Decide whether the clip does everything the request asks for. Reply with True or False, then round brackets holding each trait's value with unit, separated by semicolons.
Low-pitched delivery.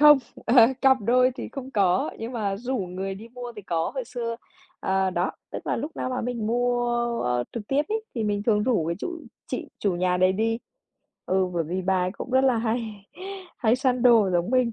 False (225 Hz)